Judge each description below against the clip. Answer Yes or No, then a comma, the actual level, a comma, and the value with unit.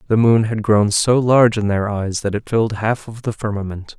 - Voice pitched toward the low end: Yes, low, 110 Hz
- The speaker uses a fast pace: Yes, fast, 240 wpm